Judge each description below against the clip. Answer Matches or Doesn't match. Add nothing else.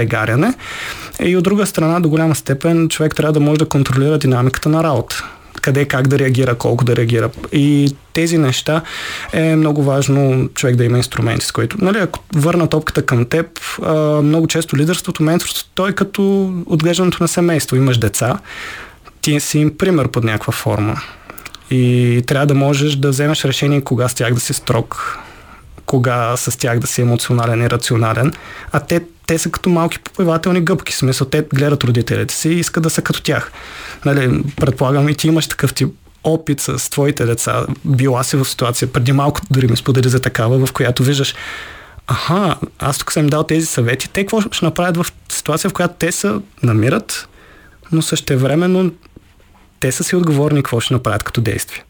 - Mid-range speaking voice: Matches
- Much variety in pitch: Doesn't match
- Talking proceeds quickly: Matches